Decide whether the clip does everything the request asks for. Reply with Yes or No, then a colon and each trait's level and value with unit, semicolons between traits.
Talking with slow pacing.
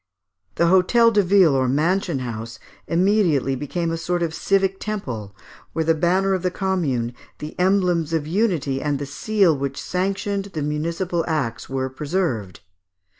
No: average, 155 wpm